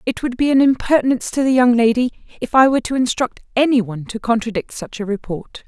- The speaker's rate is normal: No, fast, 220 wpm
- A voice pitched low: No, high, 240 Hz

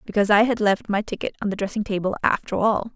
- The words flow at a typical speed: No, fast, 245 wpm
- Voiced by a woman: Yes, female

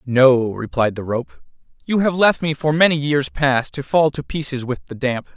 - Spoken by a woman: No, male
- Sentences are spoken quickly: Yes, fast, 215 wpm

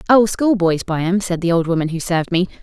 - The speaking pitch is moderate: Yes, medium, 180 Hz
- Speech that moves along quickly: Yes, fast, 250 wpm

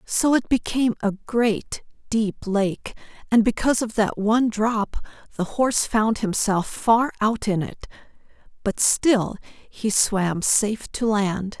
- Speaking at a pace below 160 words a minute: Yes, average, 145 wpm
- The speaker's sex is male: No, female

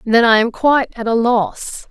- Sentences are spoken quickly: Yes, fast, 220 wpm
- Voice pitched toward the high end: Yes, high, 235 Hz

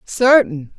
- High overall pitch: Yes, high, 205 Hz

